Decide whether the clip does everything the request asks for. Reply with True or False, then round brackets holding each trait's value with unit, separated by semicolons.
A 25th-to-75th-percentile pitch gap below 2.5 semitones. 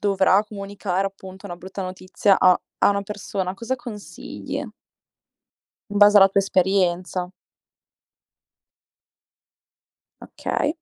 True (1.6 semitones)